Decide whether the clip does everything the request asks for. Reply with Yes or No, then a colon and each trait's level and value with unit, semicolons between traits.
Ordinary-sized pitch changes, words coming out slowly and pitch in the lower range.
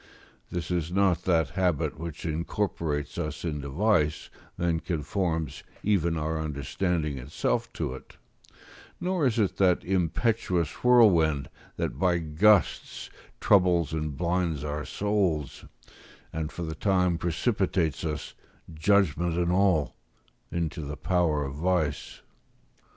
Yes: average, 3.3 semitones; slow, 120 wpm; very low, 85 Hz